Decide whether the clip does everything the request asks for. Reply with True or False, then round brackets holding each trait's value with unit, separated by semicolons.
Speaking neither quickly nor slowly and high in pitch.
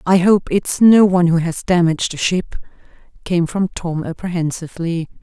False (160 wpm; 175 Hz)